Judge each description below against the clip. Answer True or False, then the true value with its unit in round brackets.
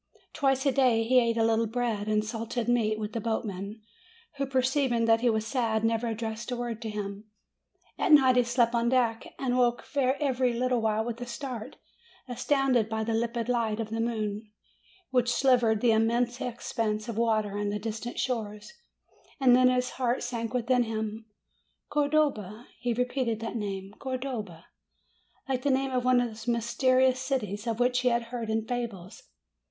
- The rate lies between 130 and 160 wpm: False (180 wpm)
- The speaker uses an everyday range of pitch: False (2.3 semitones)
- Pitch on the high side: True (235 Hz)